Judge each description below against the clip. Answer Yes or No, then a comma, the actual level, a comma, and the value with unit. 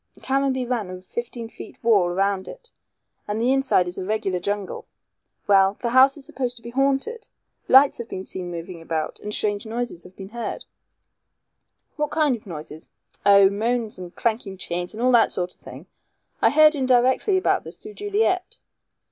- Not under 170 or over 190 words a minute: Yes, average, 180 wpm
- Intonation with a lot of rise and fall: Yes, wide, 5.7 semitones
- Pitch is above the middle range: Yes, high, 225 Hz